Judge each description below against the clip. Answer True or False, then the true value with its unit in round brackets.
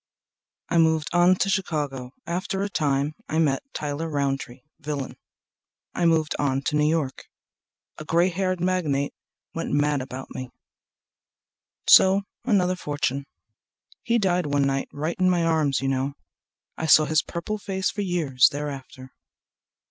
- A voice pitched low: False (155 Hz)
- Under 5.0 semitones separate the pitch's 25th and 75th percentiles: True (4.2 semitones)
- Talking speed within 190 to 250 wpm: False (140 wpm)